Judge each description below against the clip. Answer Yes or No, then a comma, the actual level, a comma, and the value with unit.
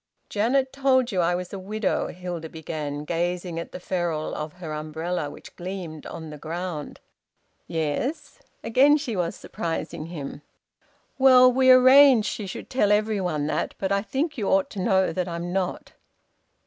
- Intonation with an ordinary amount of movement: No, wide, 5.8 semitones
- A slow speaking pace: No, average, 165 wpm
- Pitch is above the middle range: No, medium, 180 Hz